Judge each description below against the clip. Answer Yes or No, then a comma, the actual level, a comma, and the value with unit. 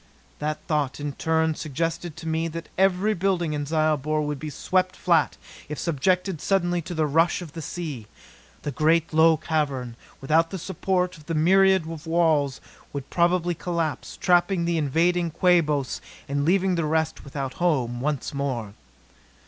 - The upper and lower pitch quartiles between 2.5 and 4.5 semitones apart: Yes, average, 3.0 semitones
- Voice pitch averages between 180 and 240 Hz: No, medium, 160 Hz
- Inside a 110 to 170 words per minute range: Yes, average, 160 wpm